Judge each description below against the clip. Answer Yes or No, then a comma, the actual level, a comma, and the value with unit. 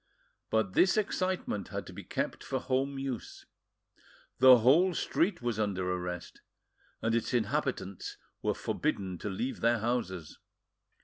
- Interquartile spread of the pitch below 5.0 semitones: No, wide, 5.6 semitones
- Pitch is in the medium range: No, low, 115 Hz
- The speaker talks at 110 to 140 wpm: Yes, slow, 135 wpm